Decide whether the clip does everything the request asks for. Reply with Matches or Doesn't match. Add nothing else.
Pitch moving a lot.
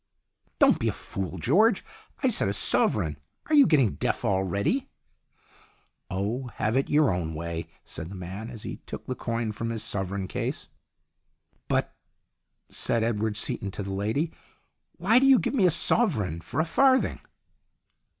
Matches